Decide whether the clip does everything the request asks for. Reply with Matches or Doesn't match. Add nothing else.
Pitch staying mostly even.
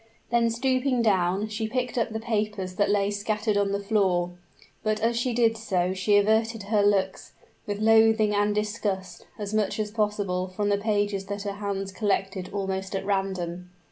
Matches